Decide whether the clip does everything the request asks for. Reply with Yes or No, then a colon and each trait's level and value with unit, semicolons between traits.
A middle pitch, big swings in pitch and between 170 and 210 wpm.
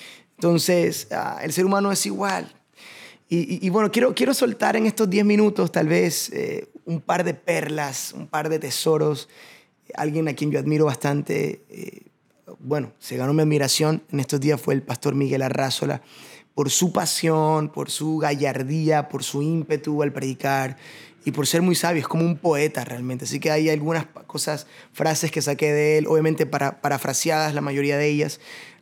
No: medium, 155 Hz; narrow, 2.6 semitones; average, 180 wpm